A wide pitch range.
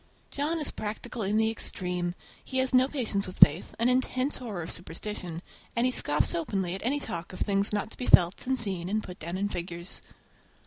Yes: wide, 5.9 semitones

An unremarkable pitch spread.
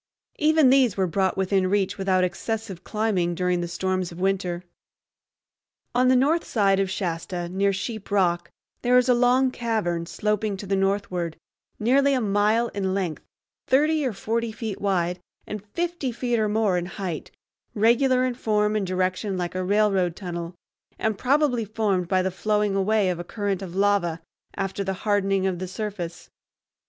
Yes: average, 3.4 semitones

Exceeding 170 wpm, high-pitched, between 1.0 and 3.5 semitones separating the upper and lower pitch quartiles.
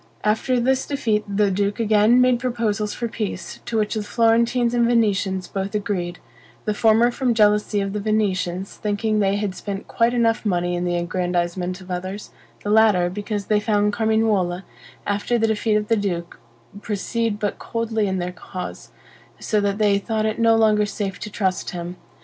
Yes: average, 180 wpm; high, 210 Hz; average, 2.7 semitones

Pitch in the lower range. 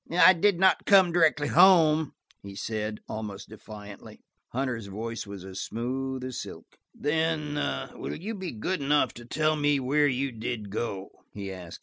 Yes: low, 130 Hz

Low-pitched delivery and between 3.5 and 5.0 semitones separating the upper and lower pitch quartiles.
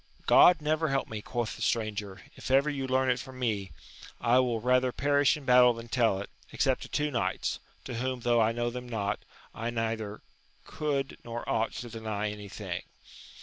No: low, 120 Hz; average, 2.8 semitones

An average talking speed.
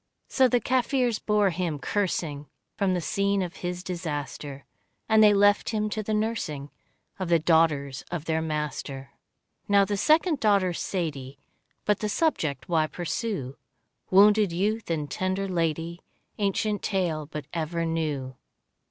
Yes: average, 145 wpm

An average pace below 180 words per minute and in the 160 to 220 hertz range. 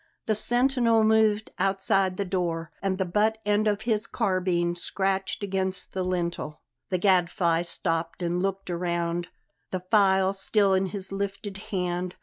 Yes: average, 145 wpm; high, 190 Hz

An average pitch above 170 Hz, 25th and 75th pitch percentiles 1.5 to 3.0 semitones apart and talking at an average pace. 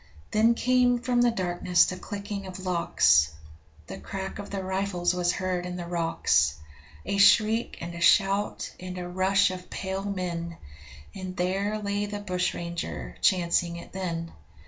Yes: medium, 185 Hz; narrow, 2.4 semitones; average, 155 wpm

